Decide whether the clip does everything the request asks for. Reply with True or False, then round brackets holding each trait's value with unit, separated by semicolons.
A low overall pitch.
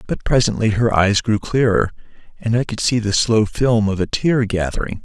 True (110 Hz)